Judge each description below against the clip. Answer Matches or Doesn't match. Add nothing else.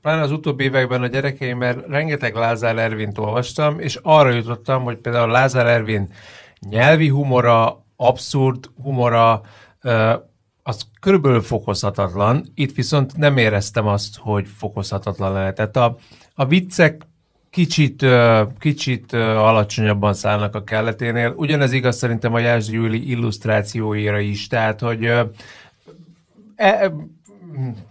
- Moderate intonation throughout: Matches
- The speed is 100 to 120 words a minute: Matches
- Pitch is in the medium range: Doesn't match